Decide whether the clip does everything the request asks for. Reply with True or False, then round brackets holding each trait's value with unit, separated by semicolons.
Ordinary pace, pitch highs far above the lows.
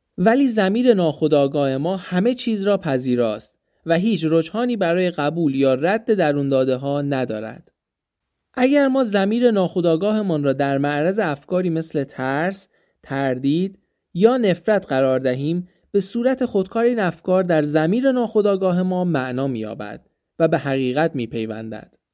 True (135 wpm; 6.8 semitones)